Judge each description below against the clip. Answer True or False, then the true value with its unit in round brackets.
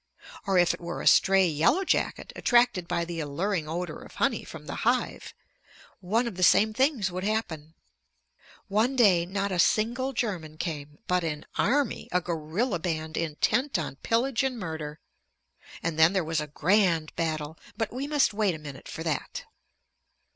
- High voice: False (180 Hz)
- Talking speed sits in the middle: True (170 wpm)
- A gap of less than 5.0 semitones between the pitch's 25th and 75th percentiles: False (5.5 semitones)